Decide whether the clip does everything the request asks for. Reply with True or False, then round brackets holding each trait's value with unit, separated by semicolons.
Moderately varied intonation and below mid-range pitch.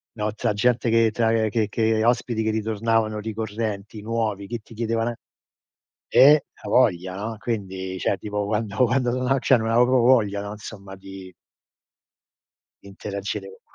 False (2.2 semitones; 110 Hz)